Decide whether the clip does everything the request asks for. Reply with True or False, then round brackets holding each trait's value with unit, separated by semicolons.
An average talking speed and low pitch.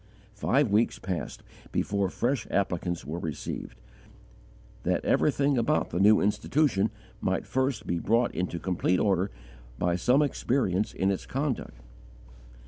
False (130 wpm; 105 Hz)